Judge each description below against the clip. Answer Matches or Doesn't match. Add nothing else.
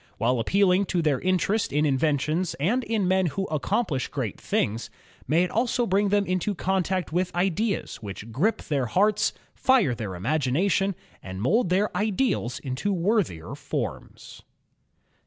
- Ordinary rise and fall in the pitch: Doesn't match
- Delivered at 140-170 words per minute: Matches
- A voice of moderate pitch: Matches